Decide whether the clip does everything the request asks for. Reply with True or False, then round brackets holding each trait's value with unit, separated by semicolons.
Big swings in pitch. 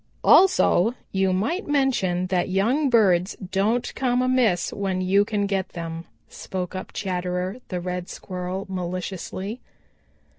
False (3.6 semitones)